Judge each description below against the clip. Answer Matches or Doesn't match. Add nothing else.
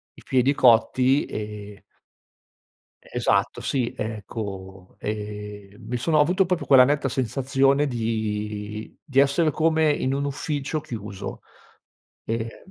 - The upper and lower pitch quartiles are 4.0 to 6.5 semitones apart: Matches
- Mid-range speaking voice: Doesn't match